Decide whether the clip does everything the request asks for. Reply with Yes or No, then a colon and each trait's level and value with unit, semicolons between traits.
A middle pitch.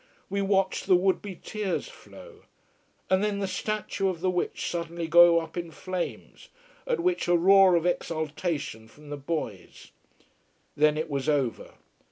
Yes: medium, 175 Hz